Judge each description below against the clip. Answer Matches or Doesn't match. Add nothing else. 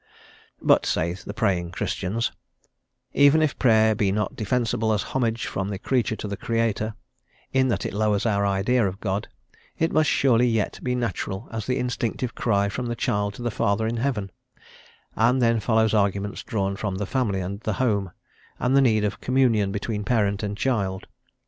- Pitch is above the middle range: Doesn't match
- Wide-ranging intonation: Doesn't match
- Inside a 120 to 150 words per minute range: Doesn't match